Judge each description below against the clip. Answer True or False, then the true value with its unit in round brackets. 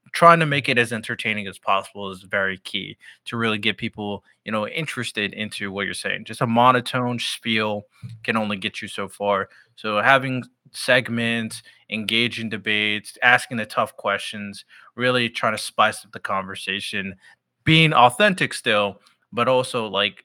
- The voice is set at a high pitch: False (115 Hz)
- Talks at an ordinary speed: True (160 wpm)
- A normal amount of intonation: True (3.3 semitones)